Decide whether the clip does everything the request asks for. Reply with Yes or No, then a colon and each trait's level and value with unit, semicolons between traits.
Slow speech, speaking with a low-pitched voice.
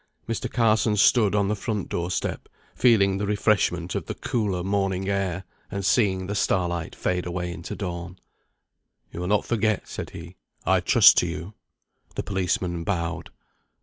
No: average, 160 wpm; very low, 95 Hz